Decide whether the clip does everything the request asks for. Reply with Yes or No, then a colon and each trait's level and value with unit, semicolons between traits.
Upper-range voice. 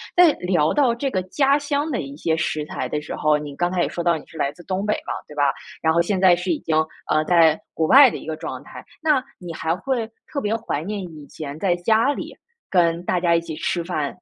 No: medium, 175 Hz